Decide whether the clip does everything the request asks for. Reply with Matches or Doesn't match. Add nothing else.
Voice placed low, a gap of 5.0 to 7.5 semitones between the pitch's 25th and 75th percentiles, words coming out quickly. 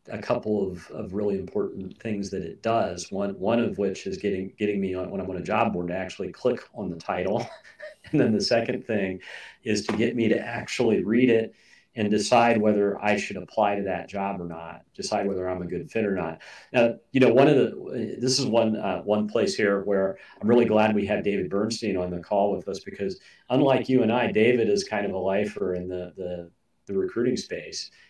Doesn't match